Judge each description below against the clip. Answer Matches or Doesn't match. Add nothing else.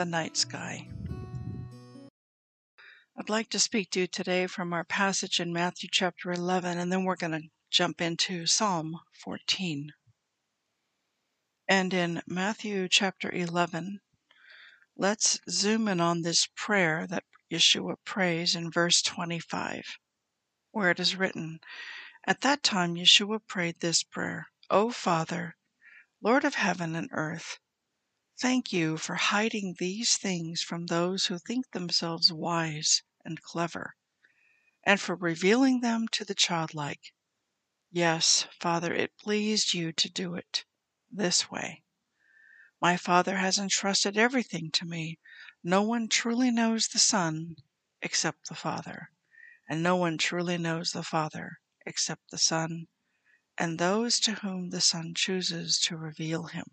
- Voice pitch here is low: Doesn't match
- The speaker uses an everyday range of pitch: Matches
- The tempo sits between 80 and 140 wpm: Matches